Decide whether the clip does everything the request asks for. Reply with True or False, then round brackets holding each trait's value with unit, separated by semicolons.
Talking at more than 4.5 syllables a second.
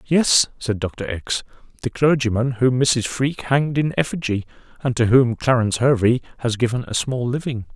True (5.1 syllables/s)